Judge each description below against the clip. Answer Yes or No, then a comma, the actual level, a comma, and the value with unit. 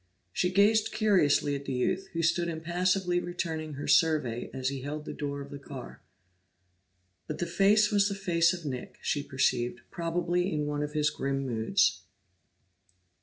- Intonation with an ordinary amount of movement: Yes, average, 4.3 semitones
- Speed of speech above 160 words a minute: Yes, average, 170 wpm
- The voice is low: No, medium, 160 Hz